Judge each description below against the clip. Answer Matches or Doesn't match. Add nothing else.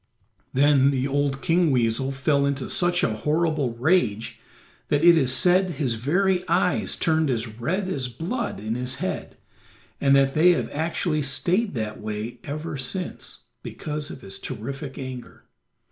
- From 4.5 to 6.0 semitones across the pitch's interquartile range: Matches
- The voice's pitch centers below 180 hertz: Matches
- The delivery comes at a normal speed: Matches